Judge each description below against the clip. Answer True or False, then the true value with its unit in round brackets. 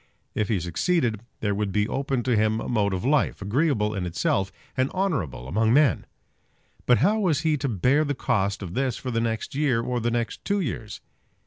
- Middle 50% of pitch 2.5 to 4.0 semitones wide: False (5.0 semitones)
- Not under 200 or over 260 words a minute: True (205 wpm)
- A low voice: True (115 Hz)